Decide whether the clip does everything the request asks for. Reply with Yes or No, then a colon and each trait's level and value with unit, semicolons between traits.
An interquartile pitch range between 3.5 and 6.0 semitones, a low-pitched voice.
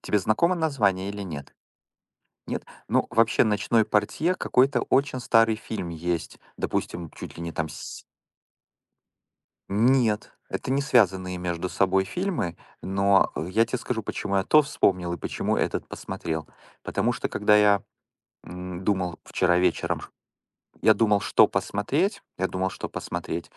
Yes: average, 4.1 semitones; low, 100 Hz